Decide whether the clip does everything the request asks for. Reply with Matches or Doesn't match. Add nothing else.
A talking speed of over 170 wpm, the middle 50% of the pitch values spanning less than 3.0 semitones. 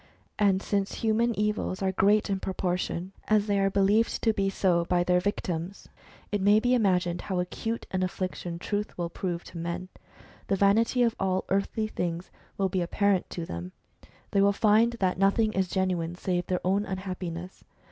Matches